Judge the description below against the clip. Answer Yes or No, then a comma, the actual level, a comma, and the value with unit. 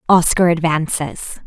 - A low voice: No, medium, 160 Hz